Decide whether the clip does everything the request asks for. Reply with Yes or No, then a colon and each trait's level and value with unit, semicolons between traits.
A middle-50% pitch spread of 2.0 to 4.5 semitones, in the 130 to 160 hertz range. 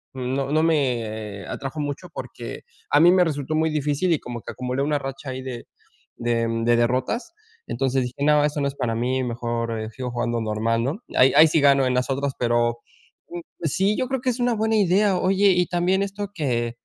No: wide, 5.5 semitones; low, 135 Hz